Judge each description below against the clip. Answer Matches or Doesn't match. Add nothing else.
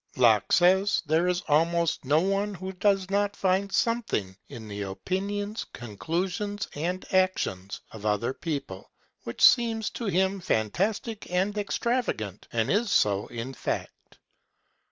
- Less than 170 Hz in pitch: Doesn't match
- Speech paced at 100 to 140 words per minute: Matches